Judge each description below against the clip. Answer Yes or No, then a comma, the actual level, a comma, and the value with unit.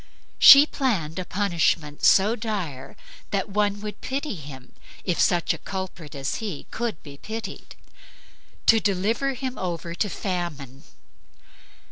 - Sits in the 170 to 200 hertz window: Yes, high, 190 Hz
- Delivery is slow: Yes, slow, 130 wpm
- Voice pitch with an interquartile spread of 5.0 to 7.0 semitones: Yes, average, 5.3 semitones